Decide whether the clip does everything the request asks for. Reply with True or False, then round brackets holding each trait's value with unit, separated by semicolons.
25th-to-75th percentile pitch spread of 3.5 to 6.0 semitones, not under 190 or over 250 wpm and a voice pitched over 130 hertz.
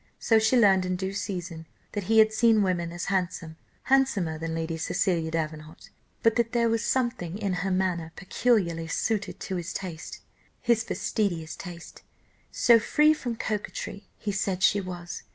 False (4.5 semitones; 165 wpm; 190 Hz)